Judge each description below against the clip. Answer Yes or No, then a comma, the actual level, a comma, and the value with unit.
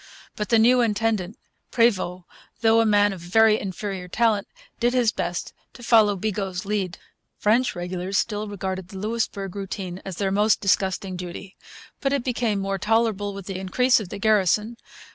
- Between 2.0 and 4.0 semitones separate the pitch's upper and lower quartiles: Yes, average, 2.8 semitones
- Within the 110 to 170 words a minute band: Yes, average, 165 wpm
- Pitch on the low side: No, high, 205 Hz